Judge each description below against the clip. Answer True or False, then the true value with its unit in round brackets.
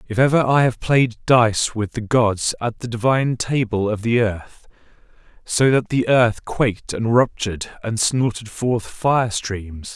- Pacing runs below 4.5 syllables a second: True (4.1 syllables/s)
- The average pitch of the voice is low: True (115 Hz)